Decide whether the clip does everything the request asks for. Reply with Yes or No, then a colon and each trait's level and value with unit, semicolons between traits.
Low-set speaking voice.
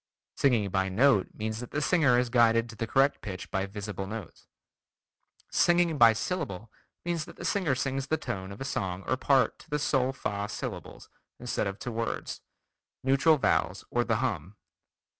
Yes: low, 120 Hz